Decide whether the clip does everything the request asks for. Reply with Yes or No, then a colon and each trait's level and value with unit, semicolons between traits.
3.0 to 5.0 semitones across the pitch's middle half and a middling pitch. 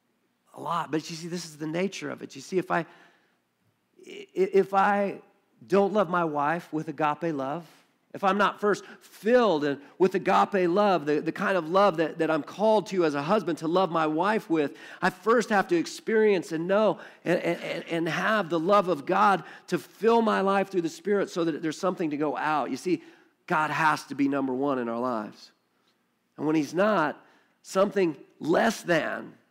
Yes: average, 4.4 semitones; medium, 180 Hz